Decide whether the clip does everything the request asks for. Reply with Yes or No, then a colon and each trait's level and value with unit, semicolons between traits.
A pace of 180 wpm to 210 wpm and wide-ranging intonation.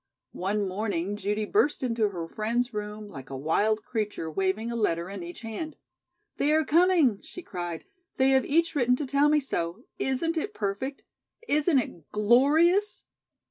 No: average, 165 wpm; wide, 6.4 semitones